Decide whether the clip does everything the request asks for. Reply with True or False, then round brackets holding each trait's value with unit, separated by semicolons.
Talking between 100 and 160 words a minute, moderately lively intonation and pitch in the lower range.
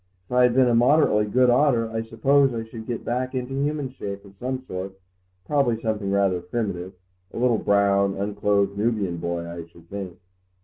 False (180 wpm; 4.3 semitones; 110 Hz)